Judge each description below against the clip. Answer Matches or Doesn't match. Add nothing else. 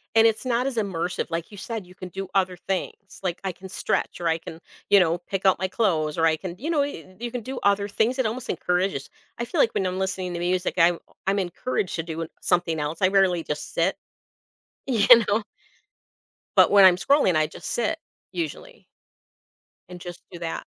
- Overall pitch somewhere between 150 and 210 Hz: Matches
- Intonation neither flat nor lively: Matches